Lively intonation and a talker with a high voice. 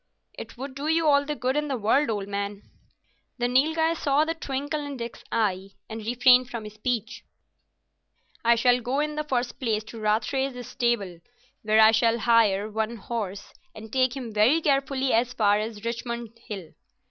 No: average, 3.9 semitones; high, 235 Hz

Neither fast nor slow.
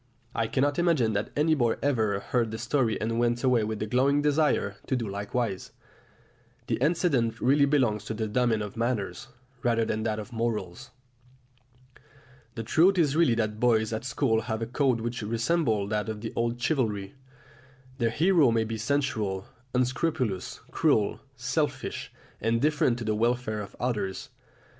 Yes: average, 160 wpm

